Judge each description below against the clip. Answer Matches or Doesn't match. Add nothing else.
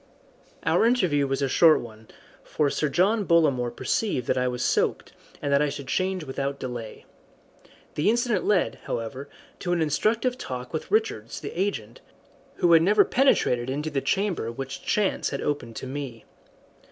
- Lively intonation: Matches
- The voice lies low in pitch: Doesn't match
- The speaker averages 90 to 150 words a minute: Doesn't match